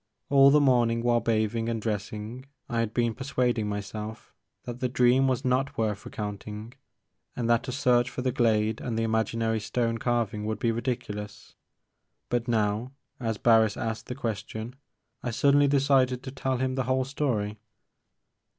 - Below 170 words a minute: Yes, average, 160 wpm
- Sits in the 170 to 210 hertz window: No, low, 120 Hz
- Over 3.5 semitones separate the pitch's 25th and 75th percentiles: No, narrow, 2.6 semitones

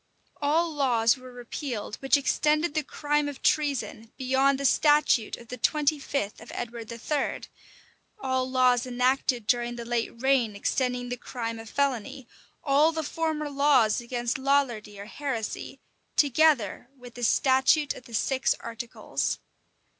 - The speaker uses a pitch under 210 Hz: No, very high, 260 Hz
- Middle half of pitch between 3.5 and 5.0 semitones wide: No, average, 3.1 semitones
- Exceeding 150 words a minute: No, average, 145 wpm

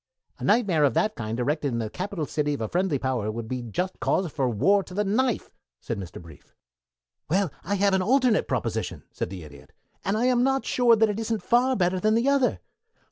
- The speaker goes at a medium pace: No, fast, 220 wpm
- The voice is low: No, medium, 185 Hz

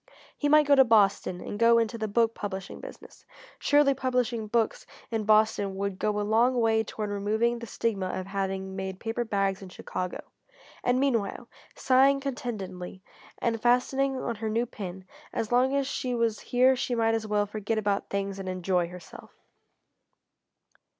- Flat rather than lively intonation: No, average, 3.7 semitones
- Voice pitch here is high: Yes, high, 220 Hz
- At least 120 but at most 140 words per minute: No, average, 170 wpm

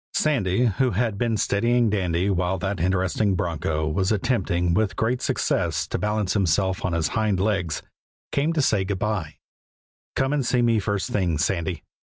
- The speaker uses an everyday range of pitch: Yes, average, 3.6 semitones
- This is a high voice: No, low, 100 Hz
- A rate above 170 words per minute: No, average, 165 wpm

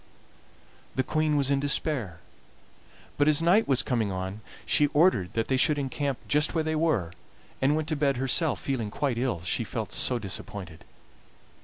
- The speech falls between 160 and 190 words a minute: Yes, average, 170 wpm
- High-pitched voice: No, low, 135 Hz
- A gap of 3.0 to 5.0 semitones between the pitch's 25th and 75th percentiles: No, wide, 5.5 semitones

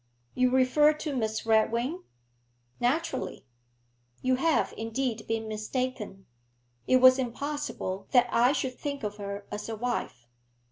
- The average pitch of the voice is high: Yes, high, 245 Hz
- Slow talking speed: Yes, slow, 130 wpm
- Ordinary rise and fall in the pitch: Yes, average, 3.4 semitones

